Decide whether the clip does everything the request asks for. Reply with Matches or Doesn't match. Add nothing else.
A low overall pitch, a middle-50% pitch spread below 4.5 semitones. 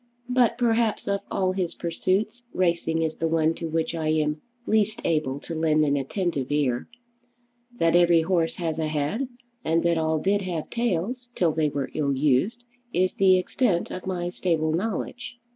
Doesn't match